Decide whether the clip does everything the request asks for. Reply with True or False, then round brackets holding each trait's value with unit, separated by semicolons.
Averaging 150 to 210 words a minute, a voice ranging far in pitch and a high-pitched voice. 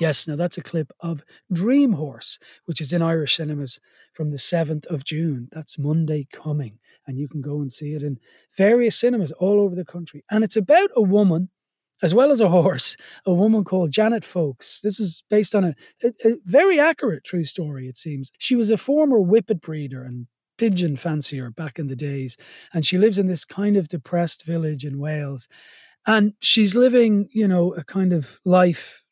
False (200 wpm; 5.8 semitones; 175 Hz)